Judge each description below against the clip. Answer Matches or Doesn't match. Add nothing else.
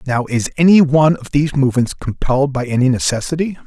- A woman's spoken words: Doesn't match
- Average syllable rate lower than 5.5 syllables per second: Doesn't match